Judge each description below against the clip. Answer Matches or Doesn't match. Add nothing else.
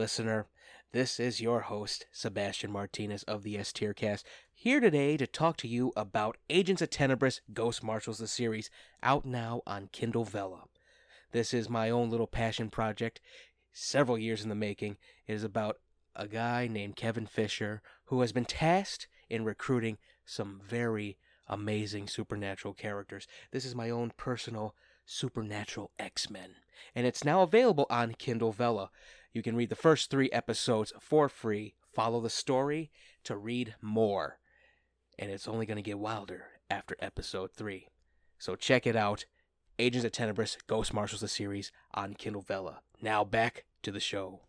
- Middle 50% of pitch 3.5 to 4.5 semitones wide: Doesn't match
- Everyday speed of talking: Matches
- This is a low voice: Matches